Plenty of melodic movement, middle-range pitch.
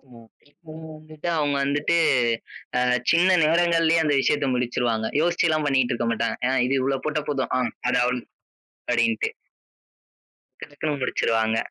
No: average, 4.2 semitones; medium, 145 Hz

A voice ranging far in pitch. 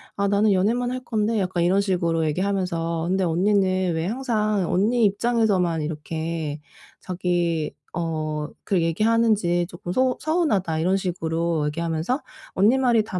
No: average, 4.3 semitones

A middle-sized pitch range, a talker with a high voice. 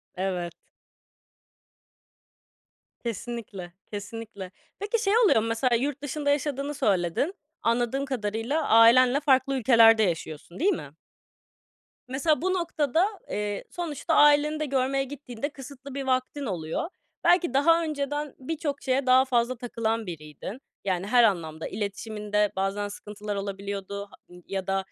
No: wide, 5.9 semitones; high, 240 Hz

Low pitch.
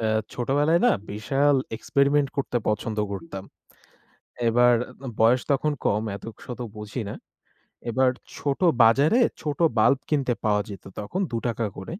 Yes: low, 125 Hz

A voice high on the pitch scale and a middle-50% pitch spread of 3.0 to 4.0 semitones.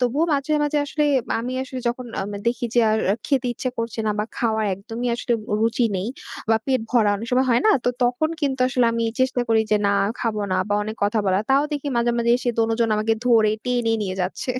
No: high, 235 Hz; narrow, 2.6 semitones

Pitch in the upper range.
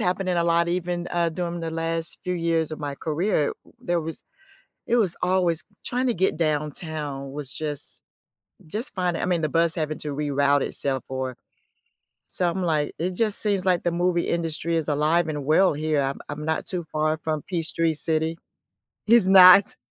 No: medium, 165 Hz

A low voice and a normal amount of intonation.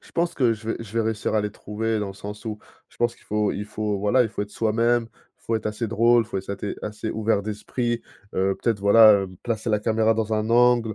No: low, 110 Hz; narrow, 1.7 semitones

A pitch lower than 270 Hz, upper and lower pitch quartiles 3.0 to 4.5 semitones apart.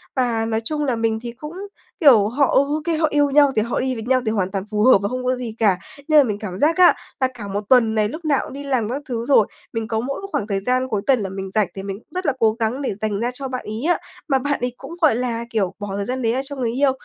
Yes: high, 245 Hz; average, 4.1 semitones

